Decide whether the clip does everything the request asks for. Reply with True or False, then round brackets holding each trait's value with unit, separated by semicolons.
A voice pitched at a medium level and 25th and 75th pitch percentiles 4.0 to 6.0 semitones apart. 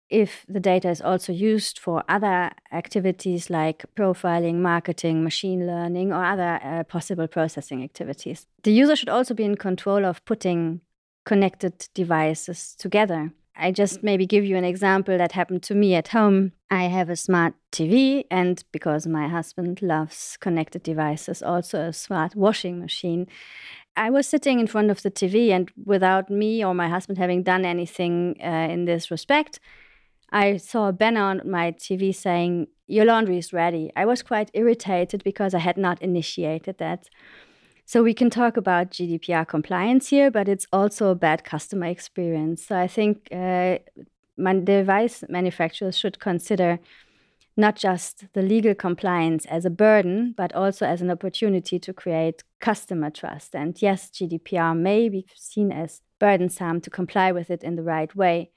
False (180 Hz; 2.9 semitones)